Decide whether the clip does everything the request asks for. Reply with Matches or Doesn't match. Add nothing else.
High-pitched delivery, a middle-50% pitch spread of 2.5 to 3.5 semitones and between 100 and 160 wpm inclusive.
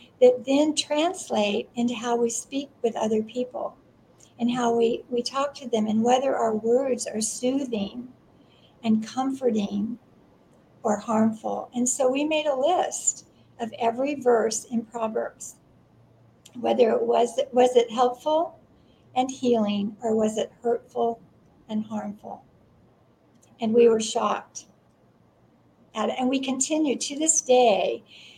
Matches